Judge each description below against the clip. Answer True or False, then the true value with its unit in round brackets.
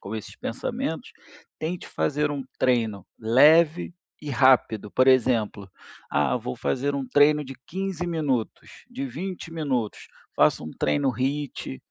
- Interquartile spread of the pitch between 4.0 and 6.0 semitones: True (4.6 semitones)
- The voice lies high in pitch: False (135 Hz)